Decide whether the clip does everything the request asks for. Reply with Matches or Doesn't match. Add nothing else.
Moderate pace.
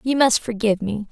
Doesn't match